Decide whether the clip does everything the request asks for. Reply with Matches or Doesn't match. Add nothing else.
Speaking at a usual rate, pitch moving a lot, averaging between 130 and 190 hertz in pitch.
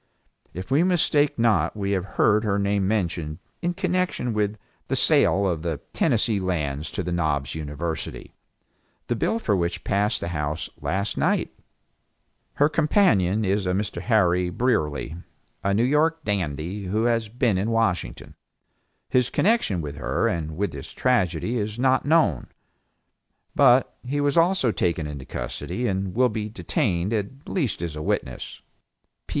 Doesn't match